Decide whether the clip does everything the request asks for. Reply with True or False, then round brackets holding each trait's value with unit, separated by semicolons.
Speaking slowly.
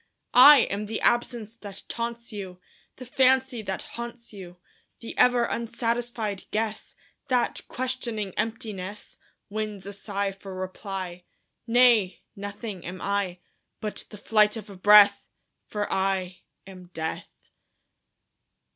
True (120 wpm)